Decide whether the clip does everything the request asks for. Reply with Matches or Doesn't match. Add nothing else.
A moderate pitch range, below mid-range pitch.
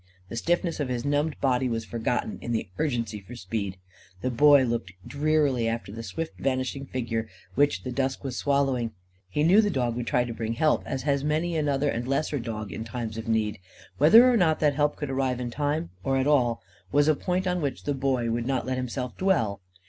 Matches